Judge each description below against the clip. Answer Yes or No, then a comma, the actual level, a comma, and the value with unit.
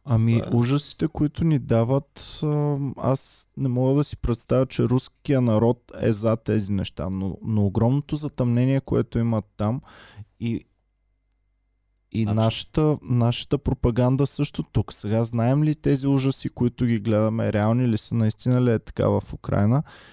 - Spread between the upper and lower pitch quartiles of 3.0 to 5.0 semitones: Yes, average, 3.8 semitones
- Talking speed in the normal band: Yes, average, 145 wpm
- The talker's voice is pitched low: Yes, low, 120 Hz